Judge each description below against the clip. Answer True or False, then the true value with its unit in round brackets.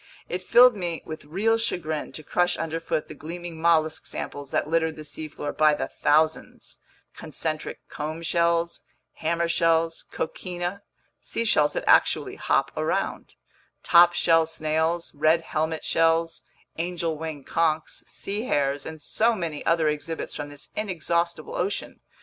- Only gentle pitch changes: True (1.8 semitones)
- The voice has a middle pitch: True (165 Hz)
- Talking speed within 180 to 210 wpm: False (140 wpm)